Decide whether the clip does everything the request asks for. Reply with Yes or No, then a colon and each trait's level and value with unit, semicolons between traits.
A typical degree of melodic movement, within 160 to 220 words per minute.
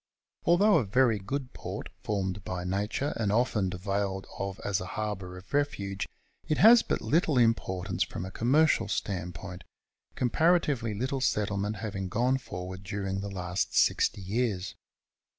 No: average, 4.9 semitones; average, 150 wpm